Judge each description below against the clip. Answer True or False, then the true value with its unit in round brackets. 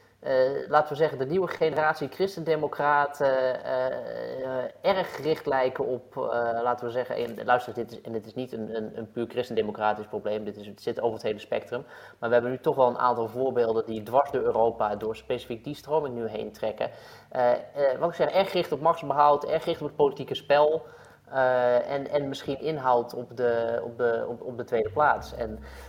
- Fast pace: True (215 wpm)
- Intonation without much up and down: False (4.1 semitones)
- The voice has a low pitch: True (130 Hz)